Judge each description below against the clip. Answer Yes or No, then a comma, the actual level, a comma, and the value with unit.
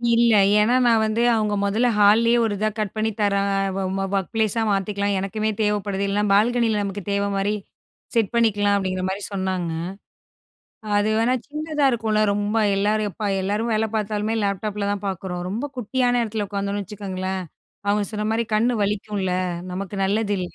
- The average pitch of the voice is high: Yes, high, 210 Hz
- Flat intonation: Yes, narrow, 1.9 semitones